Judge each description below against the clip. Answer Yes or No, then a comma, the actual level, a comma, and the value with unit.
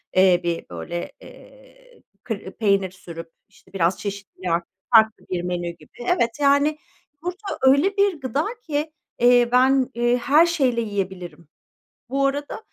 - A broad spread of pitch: Yes, wide, 7.6 semitones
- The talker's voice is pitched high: Yes, high, 240 Hz